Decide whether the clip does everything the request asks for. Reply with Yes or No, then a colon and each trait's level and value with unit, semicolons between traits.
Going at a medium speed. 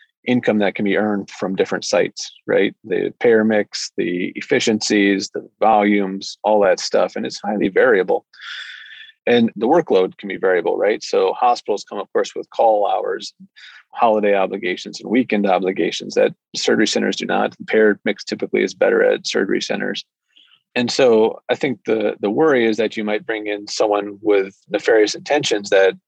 Yes: average, 175 wpm